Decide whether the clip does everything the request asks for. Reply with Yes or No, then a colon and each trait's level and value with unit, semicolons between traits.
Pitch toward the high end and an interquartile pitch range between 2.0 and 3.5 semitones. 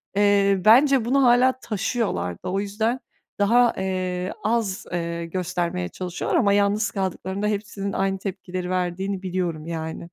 Yes: high, 195 Hz; average, 2.8 semitones